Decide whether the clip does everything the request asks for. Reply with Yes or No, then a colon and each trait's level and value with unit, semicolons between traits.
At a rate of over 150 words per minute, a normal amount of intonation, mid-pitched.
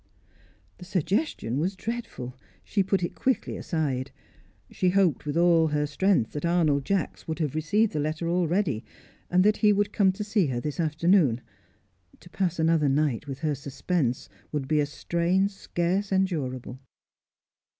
Yes: average, 160 wpm; average, 4.7 semitones; medium, 165 Hz